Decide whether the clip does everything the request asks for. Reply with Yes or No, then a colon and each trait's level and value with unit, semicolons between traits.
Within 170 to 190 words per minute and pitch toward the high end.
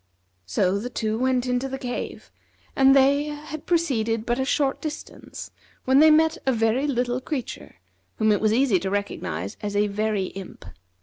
Yes: average, 175 wpm; high, 245 Hz